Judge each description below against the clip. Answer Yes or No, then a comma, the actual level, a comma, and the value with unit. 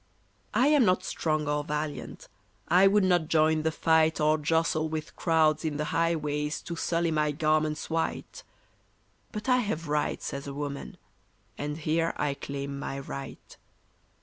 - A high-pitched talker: No, medium, 155 Hz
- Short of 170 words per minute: Yes, average, 155 wpm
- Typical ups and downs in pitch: No, narrow, 1.9 semitones